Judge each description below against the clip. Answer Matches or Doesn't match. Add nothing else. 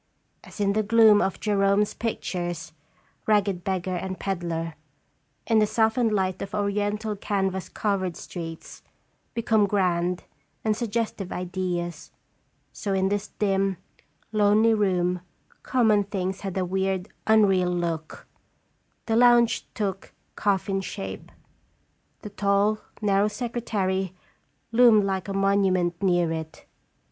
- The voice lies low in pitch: Doesn't match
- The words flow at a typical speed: Doesn't match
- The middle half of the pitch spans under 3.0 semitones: Matches